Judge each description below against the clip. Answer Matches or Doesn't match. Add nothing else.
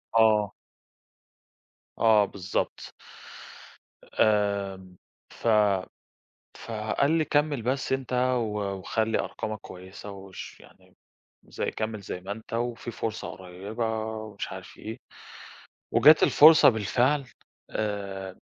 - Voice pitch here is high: Doesn't match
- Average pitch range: Matches